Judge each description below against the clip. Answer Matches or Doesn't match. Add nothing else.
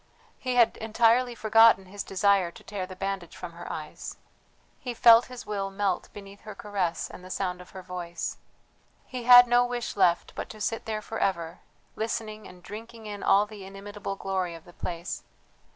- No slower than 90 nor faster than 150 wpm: Doesn't match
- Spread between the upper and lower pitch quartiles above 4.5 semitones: Doesn't match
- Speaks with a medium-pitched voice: Doesn't match